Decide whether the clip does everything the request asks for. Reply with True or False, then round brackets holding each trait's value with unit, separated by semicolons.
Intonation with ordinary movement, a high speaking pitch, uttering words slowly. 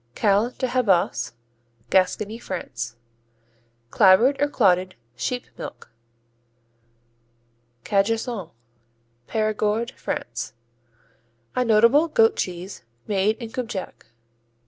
True (4.1 semitones; 210 Hz; 80 wpm)